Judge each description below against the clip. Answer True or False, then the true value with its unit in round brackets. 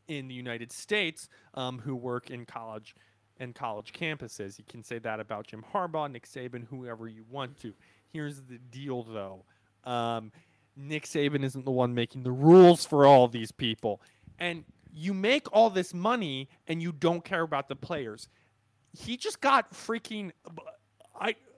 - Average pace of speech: True (165 wpm)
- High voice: False (135 Hz)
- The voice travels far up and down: True (6.1 semitones)